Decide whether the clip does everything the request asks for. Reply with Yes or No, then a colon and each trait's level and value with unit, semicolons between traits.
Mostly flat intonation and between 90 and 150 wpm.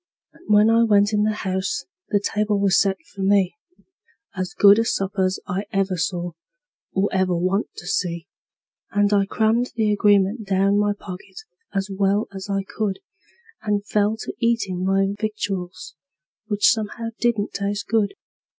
No: narrow, 1.7 semitones; average, 160 wpm